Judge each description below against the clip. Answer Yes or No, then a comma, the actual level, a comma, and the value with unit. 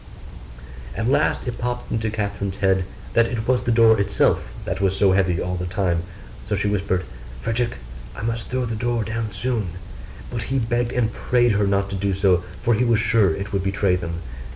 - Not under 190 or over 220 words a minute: Yes, average, 200 wpm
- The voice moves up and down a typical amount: Yes, average, 3.3 semitones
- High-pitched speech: No, low, 105 Hz